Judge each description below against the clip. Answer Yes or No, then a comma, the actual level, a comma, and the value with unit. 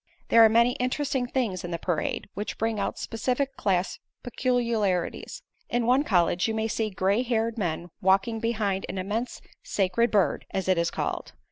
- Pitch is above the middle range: Yes, high, 220 Hz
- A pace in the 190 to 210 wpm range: No, average, 170 wpm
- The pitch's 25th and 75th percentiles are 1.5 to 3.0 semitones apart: No, average, 3.9 semitones